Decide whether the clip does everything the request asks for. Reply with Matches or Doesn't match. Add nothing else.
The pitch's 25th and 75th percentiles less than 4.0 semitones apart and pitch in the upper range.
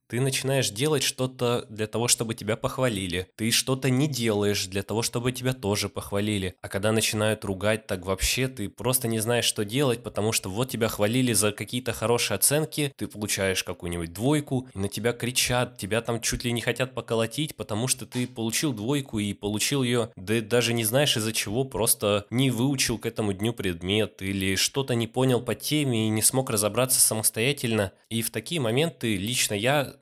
Doesn't match